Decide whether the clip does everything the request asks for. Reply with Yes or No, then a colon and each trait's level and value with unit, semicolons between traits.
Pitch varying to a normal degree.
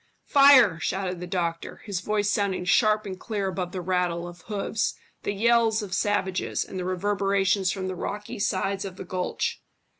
No: narrow, 2.2 semitones